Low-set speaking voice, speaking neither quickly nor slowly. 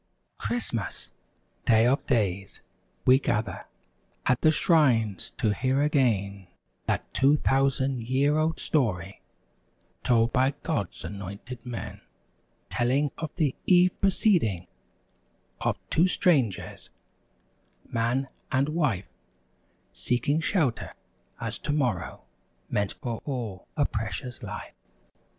No: low, 125 Hz; slow, 100 wpm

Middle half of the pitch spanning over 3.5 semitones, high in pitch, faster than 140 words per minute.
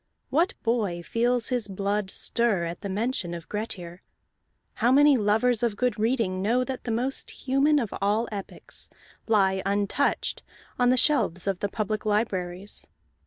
Yes: average, 4.1 semitones; high, 215 Hz; average, 155 wpm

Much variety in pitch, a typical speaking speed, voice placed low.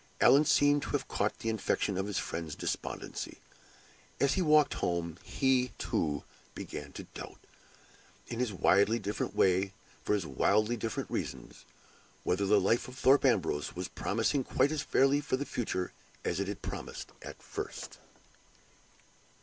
Yes: wide, 5.8 semitones; average, 160 wpm; low, 110 Hz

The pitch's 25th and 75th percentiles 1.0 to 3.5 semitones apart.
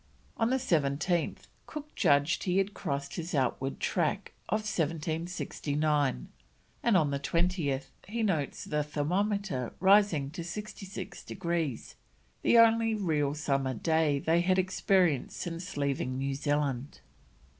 No: average, 5.1 semitones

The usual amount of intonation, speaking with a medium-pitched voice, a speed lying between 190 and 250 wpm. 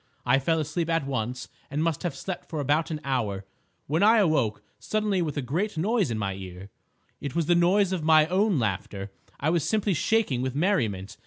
No: wide, 6.2 semitones; medium, 155 Hz; average, 200 wpm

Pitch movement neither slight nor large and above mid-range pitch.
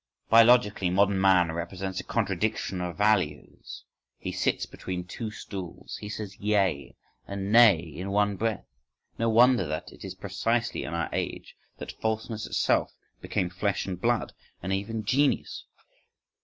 No: average, 3.4 semitones; low, 100 Hz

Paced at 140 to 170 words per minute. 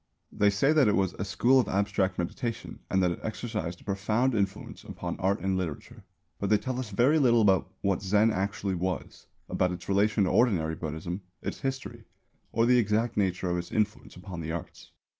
No: average, 195 wpm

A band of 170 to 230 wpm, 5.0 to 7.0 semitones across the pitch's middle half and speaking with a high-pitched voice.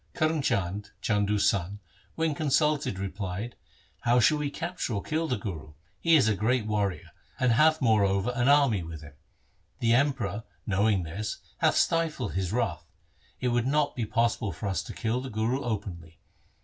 No: average, 175 wpm; wide, 5.5 semitones; low, 110 Hz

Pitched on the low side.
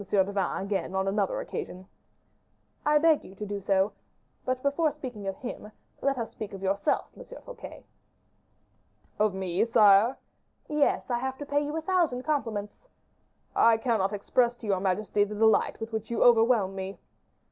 No: high, 220 Hz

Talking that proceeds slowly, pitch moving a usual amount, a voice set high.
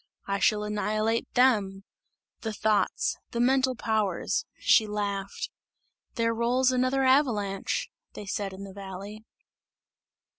Yes: slow, 115 wpm; average, 3.6 semitones; high, 215 Hz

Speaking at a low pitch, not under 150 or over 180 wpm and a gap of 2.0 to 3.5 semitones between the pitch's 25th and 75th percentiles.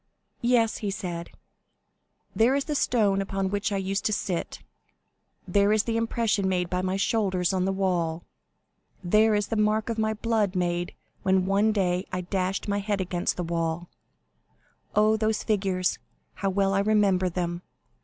No: high, 195 Hz; average, 165 wpm; average, 2.8 semitones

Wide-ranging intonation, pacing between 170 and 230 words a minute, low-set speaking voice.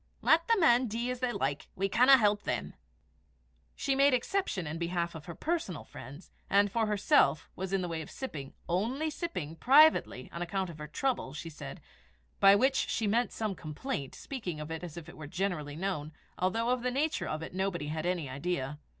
No: wide, 7.8 semitones; average, 200 wpm; high, 190 Hz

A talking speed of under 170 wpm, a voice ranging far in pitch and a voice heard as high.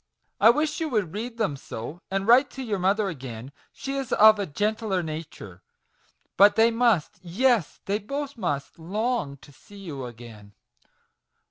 Yes: average, 160 wpm; wide, 7.4 semitones; high, 200 Hz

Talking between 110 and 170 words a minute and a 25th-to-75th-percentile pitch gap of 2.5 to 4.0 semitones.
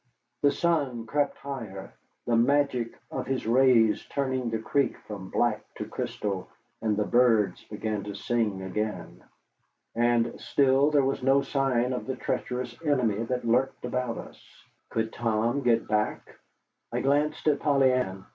Yes: average, 150 wpm; average, 3.6 semitones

